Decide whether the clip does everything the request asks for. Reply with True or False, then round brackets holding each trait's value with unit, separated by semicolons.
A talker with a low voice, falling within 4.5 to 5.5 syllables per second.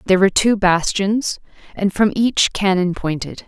False (195 Hz; 4.6 syllables/s)